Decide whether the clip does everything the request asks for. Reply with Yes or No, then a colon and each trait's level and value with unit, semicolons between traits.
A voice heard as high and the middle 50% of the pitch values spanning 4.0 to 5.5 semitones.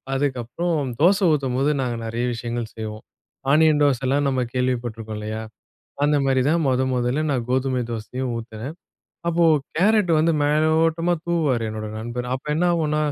No: low, 130 Hz; average, 4.6 semitones